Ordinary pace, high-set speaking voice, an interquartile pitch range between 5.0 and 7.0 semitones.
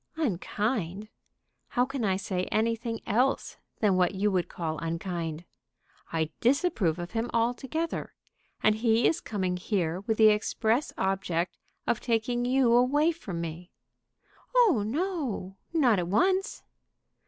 No: slow, 130 wpm; high, 215 Hz; wide, 5.4 semitones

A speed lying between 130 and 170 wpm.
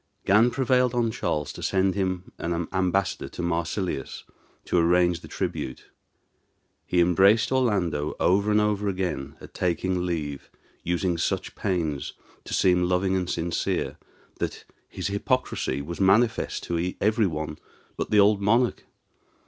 Yes: average, 140 wpm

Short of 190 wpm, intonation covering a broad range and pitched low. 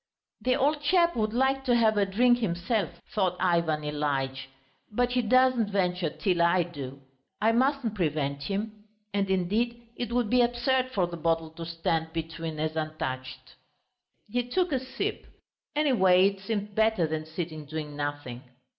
No: average, 160 wpm; wide, 7.1 semitones; high, 190 Hz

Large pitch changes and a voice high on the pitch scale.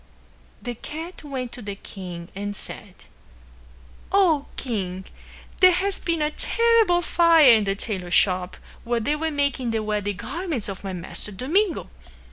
Yes: wide, 8.5 semitones; high, 245 Hz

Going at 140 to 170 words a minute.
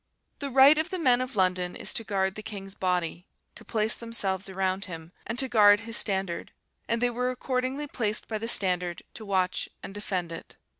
No: average, 200 wpm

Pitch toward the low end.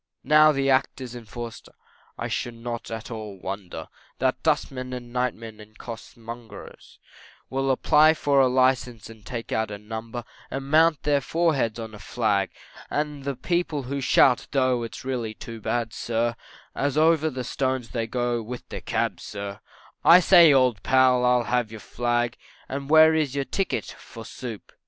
Yes: low, 125 Hz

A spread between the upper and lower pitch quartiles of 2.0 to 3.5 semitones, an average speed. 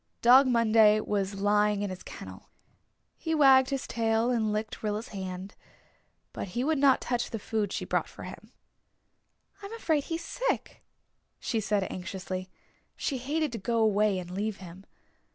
No: average, 4.5 semitones; average, 160 wpm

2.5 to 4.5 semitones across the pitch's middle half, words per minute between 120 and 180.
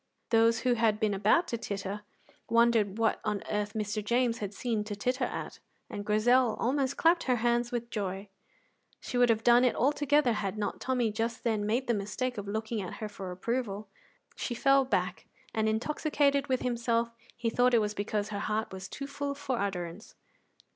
No: average, 3.1 semitones; average, 190 wpm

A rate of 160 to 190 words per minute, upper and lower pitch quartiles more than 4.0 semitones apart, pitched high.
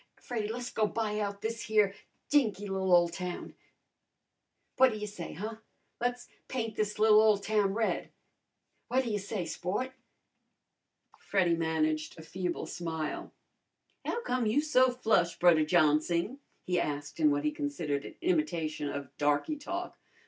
No: average, 150 wpm; wide, 5.6 semitones; high, 200 Hz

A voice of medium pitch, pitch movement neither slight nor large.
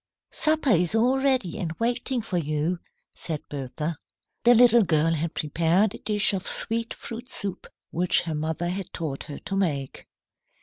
No: medium, 180 Hz; wide, 6.3 semitones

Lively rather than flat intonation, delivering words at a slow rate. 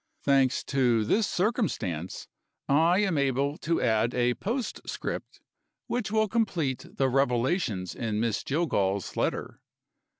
Yes: wide, 7.4 semitones; slow, 120 wpm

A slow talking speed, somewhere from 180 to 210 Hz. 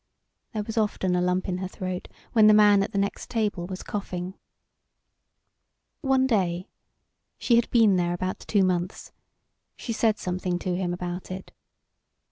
No: average, 160 wpm; high, 190 Hz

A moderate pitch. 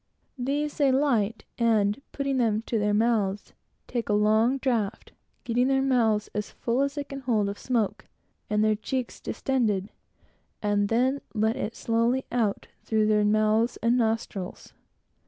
No: high, 225 Hz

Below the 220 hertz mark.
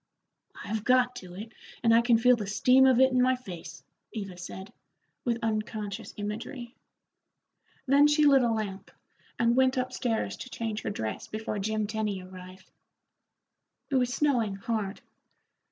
No: high, 225 Hz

